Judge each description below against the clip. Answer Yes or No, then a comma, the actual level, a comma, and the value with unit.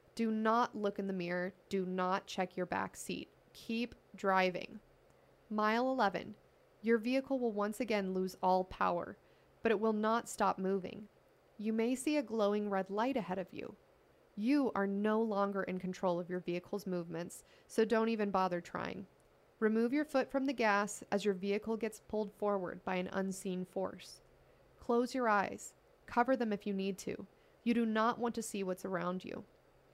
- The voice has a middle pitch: No, high, 205 Hz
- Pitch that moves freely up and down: No, average, 3.3 semitones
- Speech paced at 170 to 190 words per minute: Yes, average, 180 wpm